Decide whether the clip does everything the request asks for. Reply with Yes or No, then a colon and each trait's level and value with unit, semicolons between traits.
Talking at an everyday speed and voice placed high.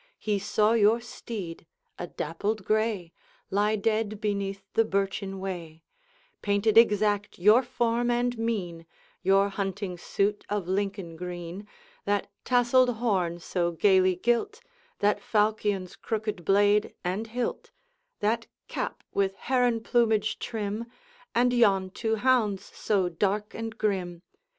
No: slow, 125 wpm; high, 205 Hz